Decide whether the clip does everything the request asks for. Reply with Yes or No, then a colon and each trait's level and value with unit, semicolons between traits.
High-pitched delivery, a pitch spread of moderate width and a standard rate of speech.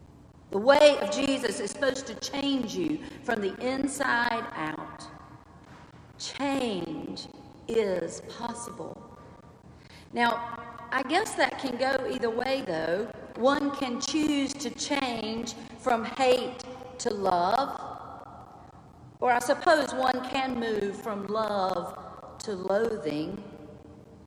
No: high, 245 Hz; average, 3.2 semitones; slow, 110 wpm